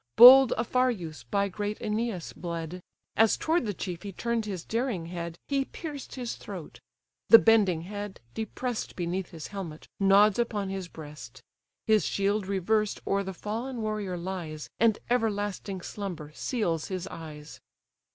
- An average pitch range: Yes, average, 4.3 semitones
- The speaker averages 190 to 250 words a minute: No, average, 145 wpm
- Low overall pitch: No, high, 200 Hz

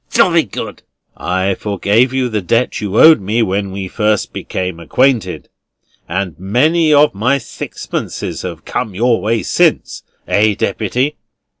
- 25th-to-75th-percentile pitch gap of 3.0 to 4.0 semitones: No, average, 4.4 semitones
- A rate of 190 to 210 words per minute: No, average, 140 wpm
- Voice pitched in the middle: No, low, 105 Hz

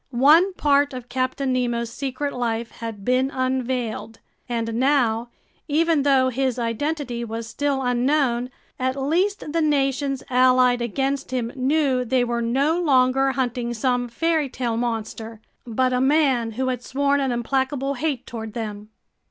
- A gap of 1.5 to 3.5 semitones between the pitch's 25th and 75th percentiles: Yes, average, 2.8 semitones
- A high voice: Yes, very high, 255 Hz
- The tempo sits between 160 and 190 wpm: No, average, 145 wpm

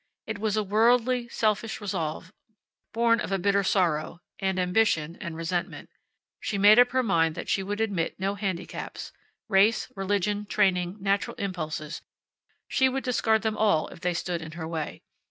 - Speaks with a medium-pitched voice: No, high, 195 Hz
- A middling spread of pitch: Yes, average, 3.8 semitones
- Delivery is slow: No, average, 165 wpm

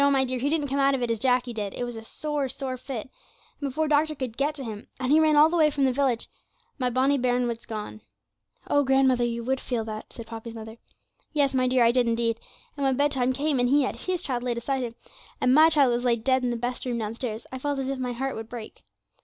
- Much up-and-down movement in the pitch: No, average, 2.8 semitones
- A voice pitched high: Yes, very high, 255 Hz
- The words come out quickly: Yes, fast, 260 wpm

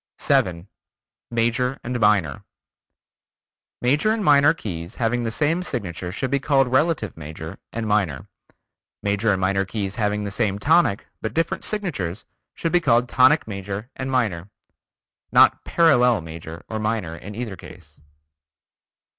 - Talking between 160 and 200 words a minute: No, average, 140 wpm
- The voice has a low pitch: Yes, low, 110 Hz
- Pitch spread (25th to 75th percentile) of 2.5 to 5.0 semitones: No, wide, 5.6 semitones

